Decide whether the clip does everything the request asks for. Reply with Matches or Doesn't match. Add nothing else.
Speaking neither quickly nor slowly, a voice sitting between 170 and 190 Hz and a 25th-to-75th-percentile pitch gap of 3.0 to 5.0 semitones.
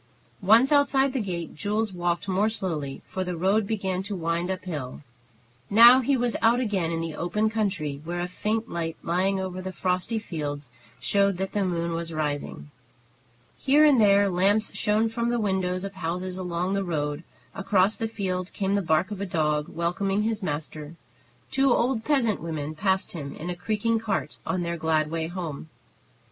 Matches